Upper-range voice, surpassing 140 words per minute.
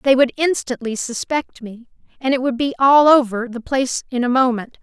Yes: very high, 255 Hz; average, 200 wpm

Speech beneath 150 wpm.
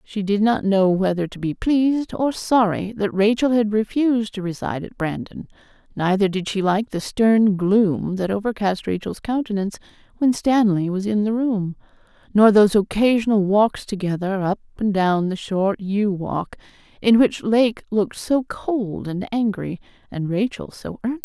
No: average, 165 wpm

